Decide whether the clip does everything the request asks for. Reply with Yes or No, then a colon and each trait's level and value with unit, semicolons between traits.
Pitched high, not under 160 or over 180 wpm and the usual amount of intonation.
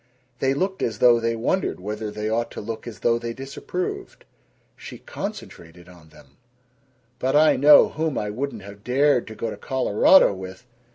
No: low, 115 Hz; average, 175 wpm; average, 4.6 semitones